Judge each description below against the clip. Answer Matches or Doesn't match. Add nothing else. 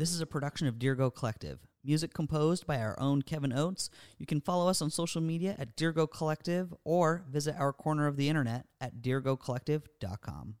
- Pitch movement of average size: Matches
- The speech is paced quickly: Doesn't match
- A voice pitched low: Doesn't match